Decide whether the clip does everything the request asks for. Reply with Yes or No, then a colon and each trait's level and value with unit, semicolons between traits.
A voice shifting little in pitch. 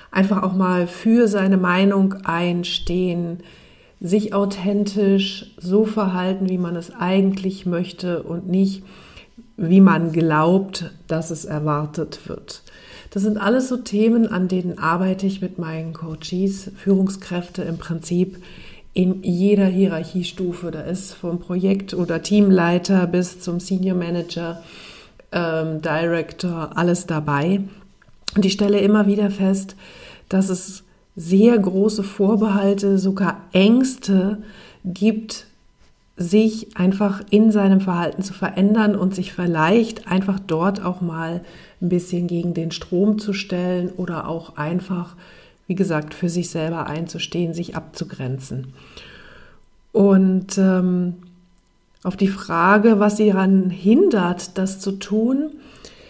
Yes: narrow, 2.3 semitones